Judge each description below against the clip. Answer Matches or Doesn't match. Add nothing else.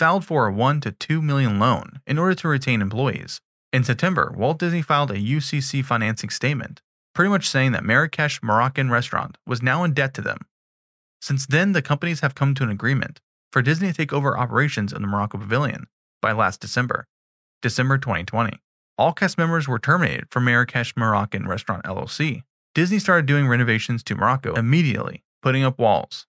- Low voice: Matches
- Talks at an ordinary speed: Matches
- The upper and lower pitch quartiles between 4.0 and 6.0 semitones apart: Matches